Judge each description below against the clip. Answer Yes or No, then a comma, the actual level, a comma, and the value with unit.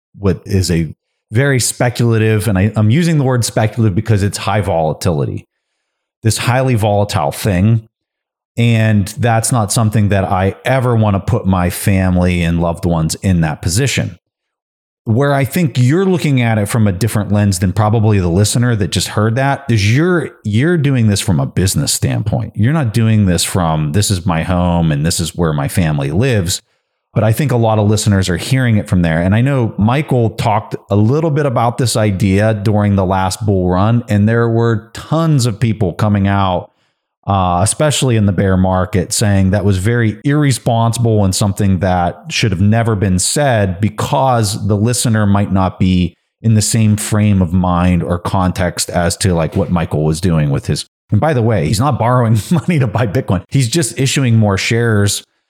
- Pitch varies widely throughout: No, average, 3.8 semitones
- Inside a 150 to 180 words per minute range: No, average, 190 wpm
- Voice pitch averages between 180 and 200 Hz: No, low, 110 Hz